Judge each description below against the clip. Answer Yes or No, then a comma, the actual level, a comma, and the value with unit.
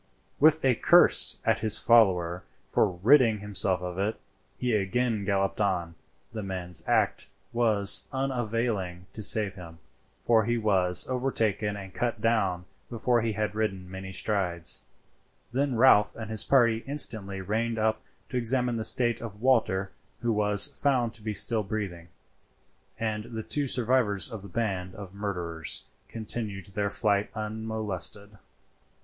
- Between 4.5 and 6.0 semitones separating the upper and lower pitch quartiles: No, average, 3.2 semitones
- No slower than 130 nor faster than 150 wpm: Yes, average, 145 wpm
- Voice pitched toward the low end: Yes, low, 105 Hz